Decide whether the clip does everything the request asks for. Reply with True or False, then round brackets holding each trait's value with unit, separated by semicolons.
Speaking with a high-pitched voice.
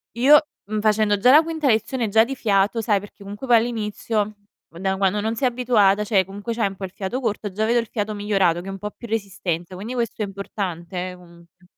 True (210 Hz)